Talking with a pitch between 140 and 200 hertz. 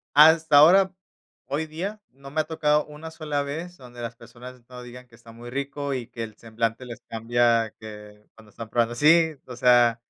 No: low, 125 Hz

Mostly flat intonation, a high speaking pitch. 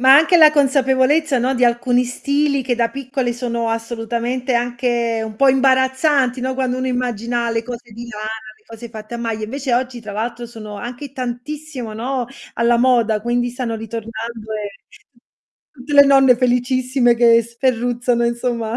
Yes: narrow, 2.0 semitones; high, 245 Hz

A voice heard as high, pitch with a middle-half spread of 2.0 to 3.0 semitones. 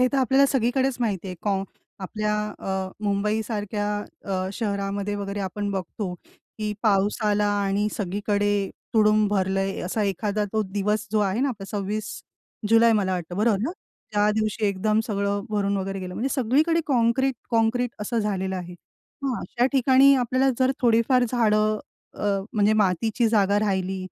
Yes: high, 210 Hz; narrow, 2.6 semitones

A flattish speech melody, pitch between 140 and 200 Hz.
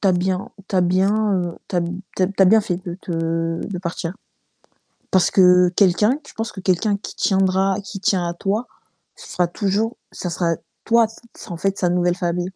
Yes: narrow, 2.2 semitones; high, 190 Hz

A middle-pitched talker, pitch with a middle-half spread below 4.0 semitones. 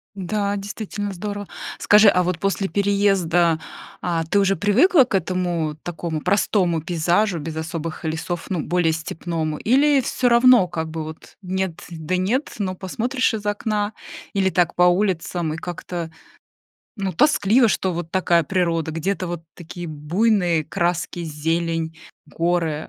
Yes: medium, 180 Hz; average, 3.6 semitones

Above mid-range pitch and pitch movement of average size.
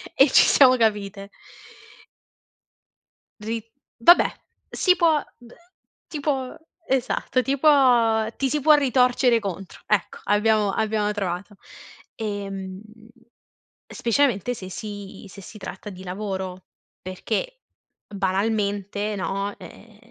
Yes: high, 215 Hz; average, 4.4 semitones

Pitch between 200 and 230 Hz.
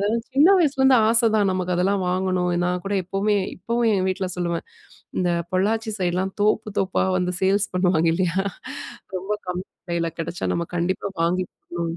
No: medium, 185 Hz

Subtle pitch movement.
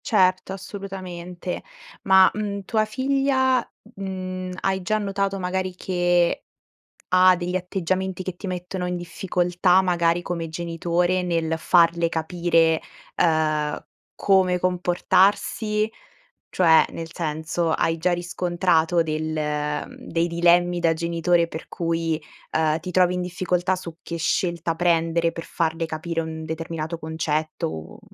Yes: narrow, 2.0 semitones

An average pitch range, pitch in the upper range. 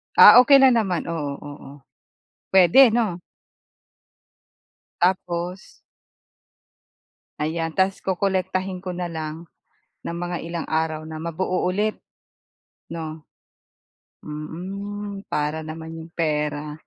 No: average, 3.1 semitones; medium, 170 Hz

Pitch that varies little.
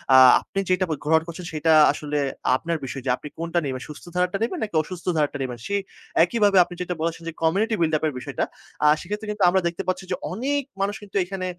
No: average, 3.7 semitones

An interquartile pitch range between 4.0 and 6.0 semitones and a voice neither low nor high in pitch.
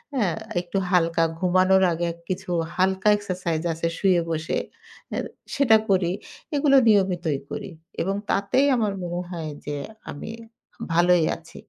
No: average, 2.7 semitones; medium, 180 Hz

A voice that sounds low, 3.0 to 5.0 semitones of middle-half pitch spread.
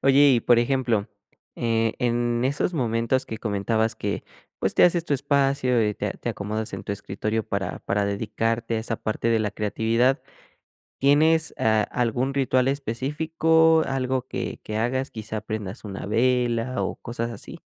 Yes: low, 120 Hz; average, 3.4 semitones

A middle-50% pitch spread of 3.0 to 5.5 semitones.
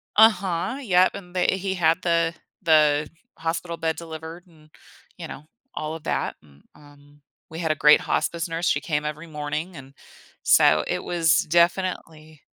No: narrow, 2.5 semitones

